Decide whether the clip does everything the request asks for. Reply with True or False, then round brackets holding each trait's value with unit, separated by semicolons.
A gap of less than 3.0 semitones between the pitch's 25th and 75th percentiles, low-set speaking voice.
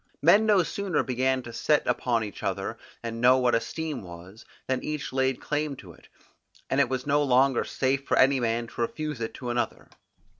False (3.8 semitones; 130 Hz)